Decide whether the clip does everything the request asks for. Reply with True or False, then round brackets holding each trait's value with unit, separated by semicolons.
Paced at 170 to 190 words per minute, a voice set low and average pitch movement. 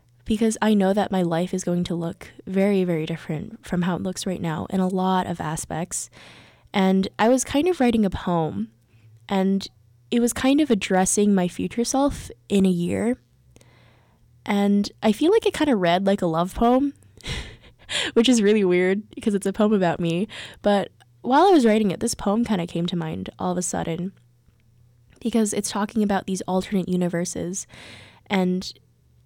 False (185 wpm; 190 Hz; 3.8 semitones)